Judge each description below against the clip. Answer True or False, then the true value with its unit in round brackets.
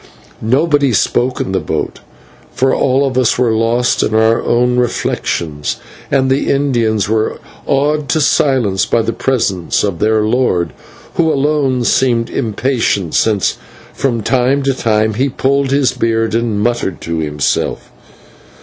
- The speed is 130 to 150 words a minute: True (145 wpm)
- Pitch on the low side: True (120 Hz)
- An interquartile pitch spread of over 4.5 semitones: False (3.7 semitones)